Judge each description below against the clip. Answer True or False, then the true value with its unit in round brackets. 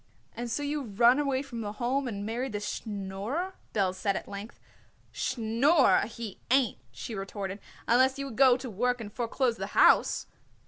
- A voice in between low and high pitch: False (235 Hz)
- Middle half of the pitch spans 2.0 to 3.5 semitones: False (4.1 semitones)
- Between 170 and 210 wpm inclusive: True (175 wpm)